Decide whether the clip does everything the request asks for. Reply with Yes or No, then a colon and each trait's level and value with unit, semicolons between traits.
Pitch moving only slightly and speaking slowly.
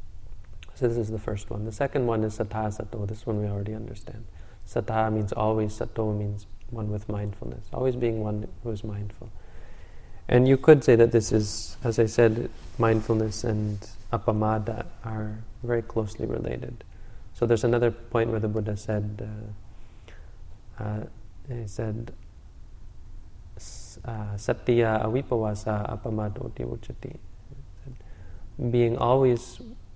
Yes: narrow, 2.2 semitones; slow, 130 wpm